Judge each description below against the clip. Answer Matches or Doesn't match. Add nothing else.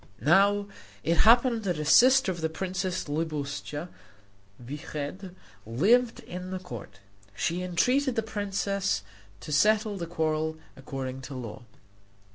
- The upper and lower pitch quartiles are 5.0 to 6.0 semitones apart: Matches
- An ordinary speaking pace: Doesn't match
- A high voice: Doesn't match